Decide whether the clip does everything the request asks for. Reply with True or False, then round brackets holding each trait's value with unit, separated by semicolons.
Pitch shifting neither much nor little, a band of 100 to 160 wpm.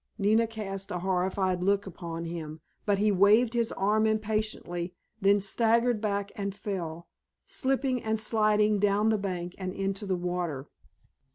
True (3.0 semitones; 150 wpm)